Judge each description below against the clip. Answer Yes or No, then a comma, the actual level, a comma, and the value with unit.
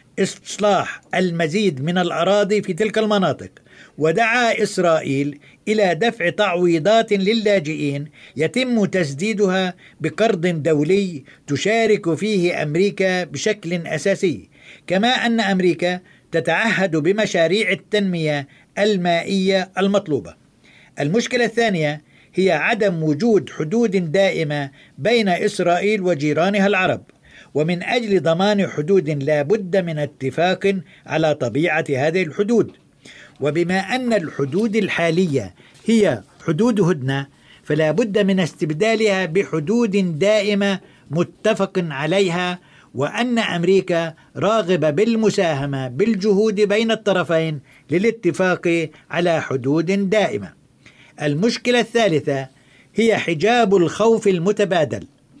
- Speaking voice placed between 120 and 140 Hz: No, medium, 185 Hz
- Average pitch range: Yes, average, 4.9 semitones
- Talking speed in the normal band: Yes, average, 90 wpm